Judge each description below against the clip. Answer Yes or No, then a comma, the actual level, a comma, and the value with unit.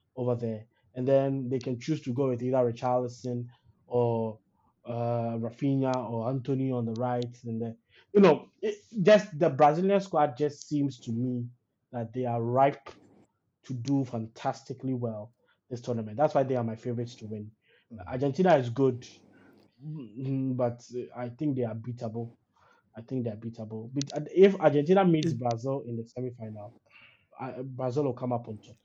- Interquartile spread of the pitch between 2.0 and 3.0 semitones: Yes, average, 2.7 semitones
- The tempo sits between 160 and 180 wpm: Yes, average, 165 wpm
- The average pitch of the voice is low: Yes, low, 125 Hz